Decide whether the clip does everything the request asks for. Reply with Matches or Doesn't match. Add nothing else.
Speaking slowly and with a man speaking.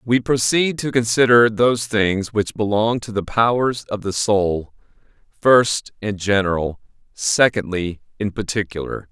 Matches